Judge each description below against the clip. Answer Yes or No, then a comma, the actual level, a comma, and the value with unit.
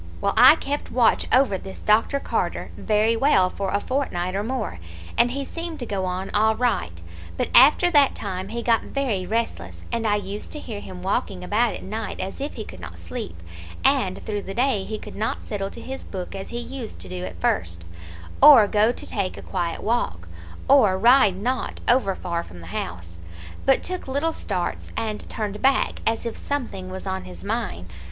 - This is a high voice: Yes, high, 215 Hz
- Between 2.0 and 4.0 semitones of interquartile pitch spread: No, average, 5.0 semitones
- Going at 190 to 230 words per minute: Yes, average, 200 wpm